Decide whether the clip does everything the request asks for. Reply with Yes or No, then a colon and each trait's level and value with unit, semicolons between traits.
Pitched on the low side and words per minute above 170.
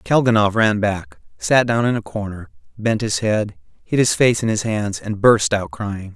Yes: low, 105 Hz; fast, 205 wpm